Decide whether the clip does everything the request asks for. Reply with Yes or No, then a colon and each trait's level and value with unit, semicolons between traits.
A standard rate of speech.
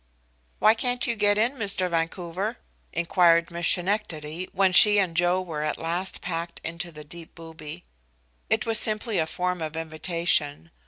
Yes: average, 160 wpm